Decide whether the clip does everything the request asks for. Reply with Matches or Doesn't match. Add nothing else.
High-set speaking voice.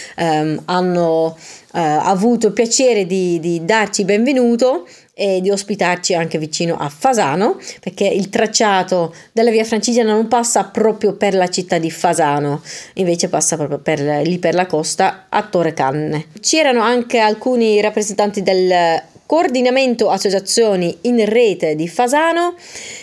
Matches